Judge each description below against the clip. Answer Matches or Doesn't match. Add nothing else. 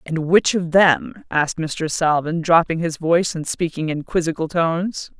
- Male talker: Doesn't match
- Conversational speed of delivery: Matches